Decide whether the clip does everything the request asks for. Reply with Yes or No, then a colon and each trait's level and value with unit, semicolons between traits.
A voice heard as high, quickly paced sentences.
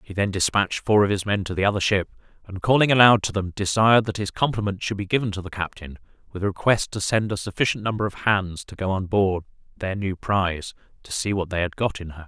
No: low, 100 Hz; fast, 250 wpm